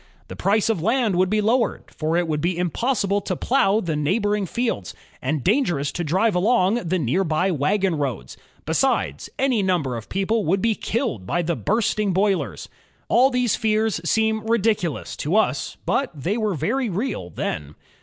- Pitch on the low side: No, high, 195 Hz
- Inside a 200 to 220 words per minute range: No, average, 180 wpm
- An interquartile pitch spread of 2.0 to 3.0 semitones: No, average, 5.3 semitones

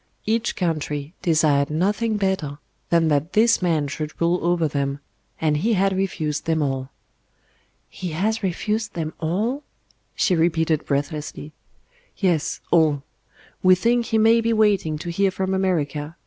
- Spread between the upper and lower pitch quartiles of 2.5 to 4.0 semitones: No, average, 4.4 semitones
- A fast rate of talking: No, average, 145 wpm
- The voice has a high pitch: No, medium, 170 Hz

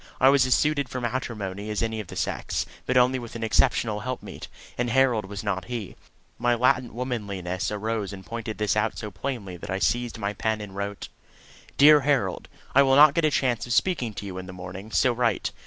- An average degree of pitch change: Yes, average, 3.9 semitones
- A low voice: Yes, low, 115 Hz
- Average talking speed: No, fast, 215 wpm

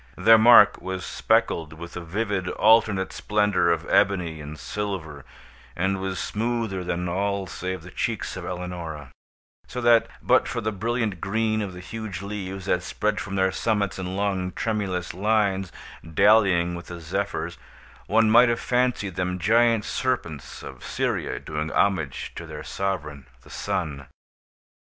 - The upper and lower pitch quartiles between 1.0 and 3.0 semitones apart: No, average, 3.4 semitones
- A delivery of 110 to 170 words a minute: Yes, average, 150 wpm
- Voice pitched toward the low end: Yes, very low, 95 Hz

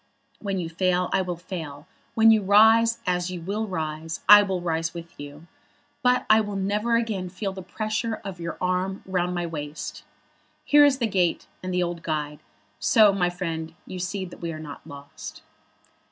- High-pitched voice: No, medium, 180 Hz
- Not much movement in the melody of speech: No, average, 3.7 semitones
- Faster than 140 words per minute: Yes, average, 185 wpm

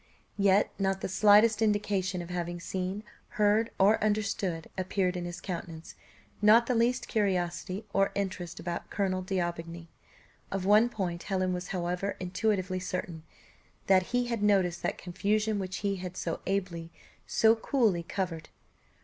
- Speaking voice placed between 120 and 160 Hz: No, high, 190 Hz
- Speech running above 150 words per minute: No, average, 145 wpm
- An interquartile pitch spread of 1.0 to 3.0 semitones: Yes, average, 2.7 semitones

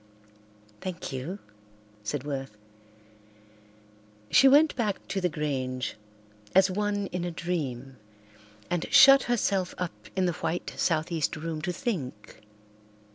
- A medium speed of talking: No, slow, 120 wpm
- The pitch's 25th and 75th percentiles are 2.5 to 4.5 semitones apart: No, average, 5.1 semitones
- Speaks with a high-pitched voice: No, medium, 175 Hz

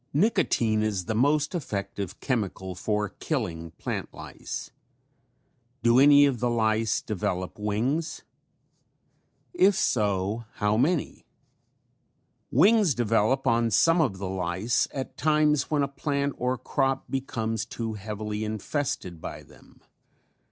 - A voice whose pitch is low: Yes, low, 115 Hz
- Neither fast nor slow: No, slow, 120 wpm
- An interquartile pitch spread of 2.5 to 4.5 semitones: No, average, 5.2 semitones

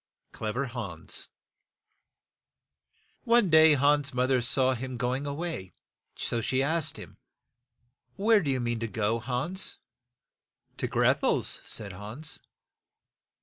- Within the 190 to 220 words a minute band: No, slow, 135 wpm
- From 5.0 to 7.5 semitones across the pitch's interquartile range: No, average, 4.5 semitones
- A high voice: No, low, 130 Hz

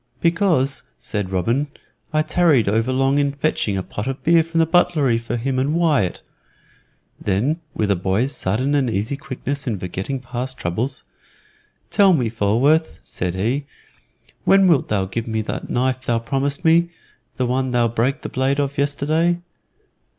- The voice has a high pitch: No, low, 130 Hz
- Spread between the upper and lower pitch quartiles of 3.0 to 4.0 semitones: No, average, 4.5 semitones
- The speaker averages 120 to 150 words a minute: No, average, 160 wpm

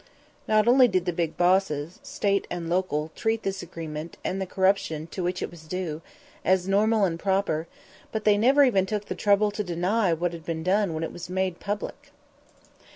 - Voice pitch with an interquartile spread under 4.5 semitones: Yes, average, 3.4 semitones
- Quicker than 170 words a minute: Yes, average, 195 wpm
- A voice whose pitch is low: No, medium, 185 Hz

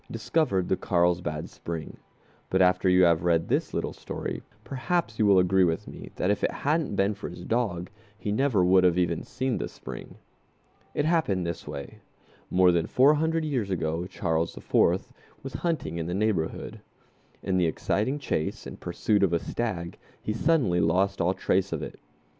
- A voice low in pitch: Yes, very low, 95 Hz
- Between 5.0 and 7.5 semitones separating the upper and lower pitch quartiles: Yes, average, 5.3 semitones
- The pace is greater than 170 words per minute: Yes, average, 180 wpm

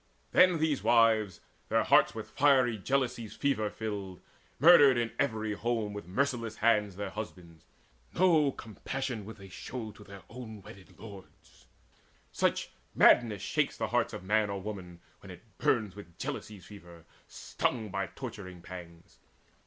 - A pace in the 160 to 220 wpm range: No, average, 145 wpm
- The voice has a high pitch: No, low, 110 Hz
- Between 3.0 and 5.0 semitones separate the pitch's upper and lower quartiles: Yes, average, 3.7 semitones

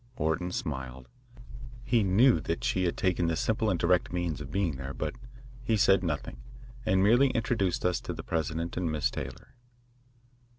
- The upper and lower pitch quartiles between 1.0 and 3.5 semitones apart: No, average, 4.0 semitones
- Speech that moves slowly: No, average, 170 wpm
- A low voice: Yes, very low, 90 Hz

